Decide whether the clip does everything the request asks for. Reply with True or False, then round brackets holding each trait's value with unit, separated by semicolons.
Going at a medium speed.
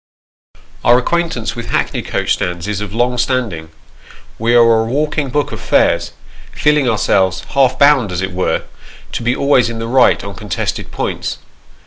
True (165 wpm)